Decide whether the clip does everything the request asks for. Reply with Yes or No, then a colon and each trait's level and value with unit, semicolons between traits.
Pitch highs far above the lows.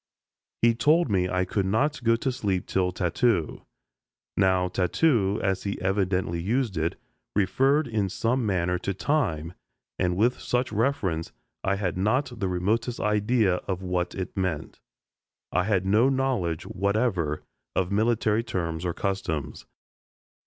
No: average, 4.3 semitones